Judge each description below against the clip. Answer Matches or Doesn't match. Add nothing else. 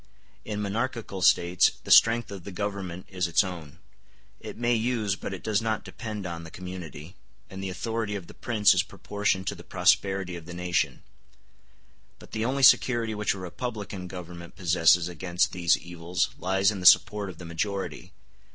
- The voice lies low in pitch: Matches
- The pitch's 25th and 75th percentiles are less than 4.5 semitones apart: Matches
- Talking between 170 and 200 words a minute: Matches